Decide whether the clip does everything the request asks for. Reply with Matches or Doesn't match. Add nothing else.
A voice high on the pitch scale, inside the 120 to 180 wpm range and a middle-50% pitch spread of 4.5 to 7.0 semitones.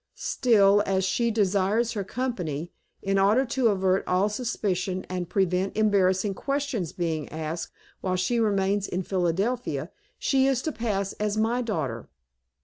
Doesn't match